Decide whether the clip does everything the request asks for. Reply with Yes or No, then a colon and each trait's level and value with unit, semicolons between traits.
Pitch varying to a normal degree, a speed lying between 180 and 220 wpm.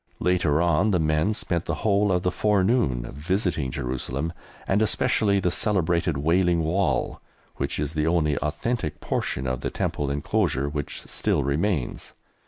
No: average, 4.8 semitones; average, 150 wpm